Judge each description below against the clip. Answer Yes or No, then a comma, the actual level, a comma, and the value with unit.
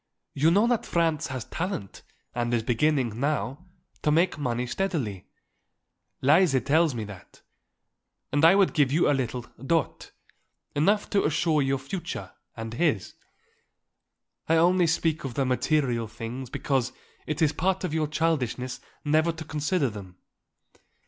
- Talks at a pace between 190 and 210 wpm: No, average, 145 wpm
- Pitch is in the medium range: Yes, medium, 145 Hz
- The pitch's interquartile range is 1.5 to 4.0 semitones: No, average, 4.8 semitones